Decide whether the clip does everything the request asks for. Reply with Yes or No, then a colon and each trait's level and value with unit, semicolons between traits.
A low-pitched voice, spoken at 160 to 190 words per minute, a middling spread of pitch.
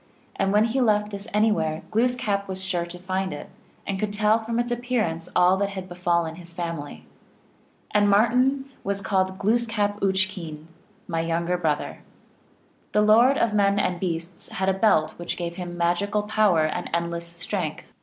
No: high, 190 Hz; average, 185 wpm; average, 3.5 semitones